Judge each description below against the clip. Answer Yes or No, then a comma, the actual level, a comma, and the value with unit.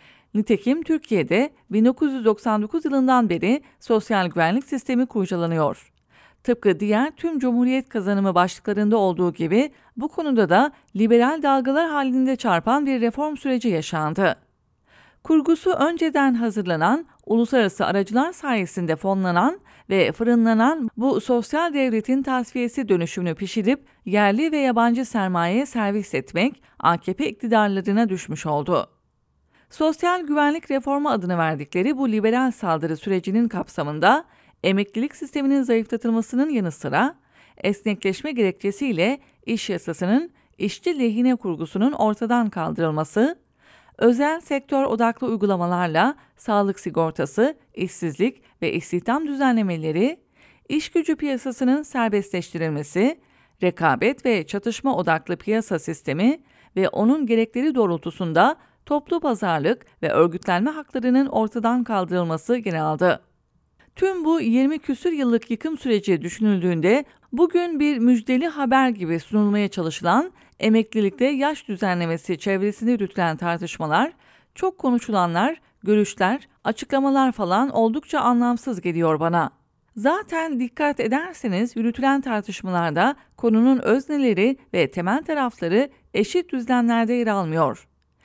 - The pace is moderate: No, slow, 105 wpm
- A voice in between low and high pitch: No, high, 230 Hz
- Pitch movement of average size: No, wide, 6.2 semitones